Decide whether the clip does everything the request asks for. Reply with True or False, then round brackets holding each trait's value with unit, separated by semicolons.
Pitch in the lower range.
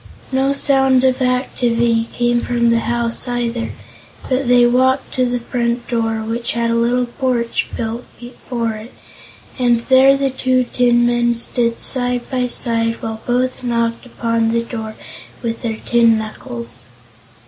False (240 Hz)